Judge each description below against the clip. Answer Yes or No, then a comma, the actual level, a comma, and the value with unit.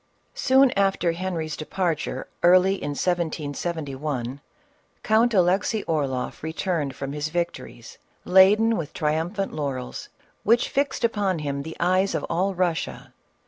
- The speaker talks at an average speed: No, slow, 120 wpm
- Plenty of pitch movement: No, average, 4.4 semitones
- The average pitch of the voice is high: No, medium, 175 Hz